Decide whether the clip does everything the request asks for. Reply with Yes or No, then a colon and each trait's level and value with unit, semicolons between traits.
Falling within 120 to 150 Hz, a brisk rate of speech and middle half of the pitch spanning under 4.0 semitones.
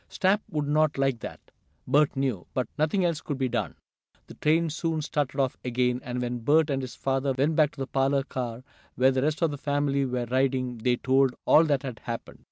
Yes: low, 135 Hz; fast, 215 wpm; average, 2.9 semitones